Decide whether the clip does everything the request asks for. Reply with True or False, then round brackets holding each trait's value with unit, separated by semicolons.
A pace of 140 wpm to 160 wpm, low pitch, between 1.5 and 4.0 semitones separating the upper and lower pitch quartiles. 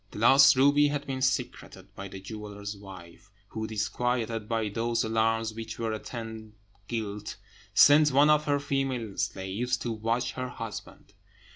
True (150 wpm; 115 Hz; 3.6 semitones)